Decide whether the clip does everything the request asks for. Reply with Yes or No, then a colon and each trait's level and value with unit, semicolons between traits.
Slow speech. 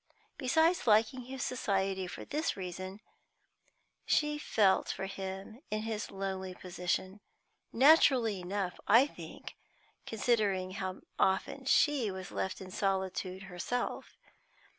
Yes: slow, 115 wpm